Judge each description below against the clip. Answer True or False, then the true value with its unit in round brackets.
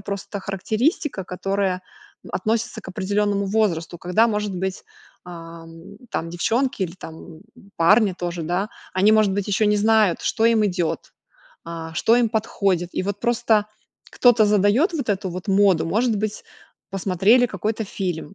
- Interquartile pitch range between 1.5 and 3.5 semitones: True (3.2 semitones)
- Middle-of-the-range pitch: False (200 Hz)